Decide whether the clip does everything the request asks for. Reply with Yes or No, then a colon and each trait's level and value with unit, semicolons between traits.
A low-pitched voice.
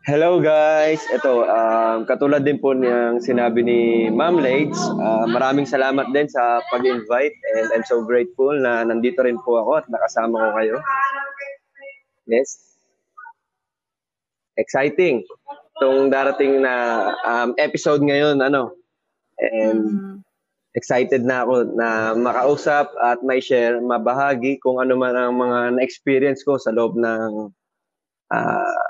Yes: low, 130 Hz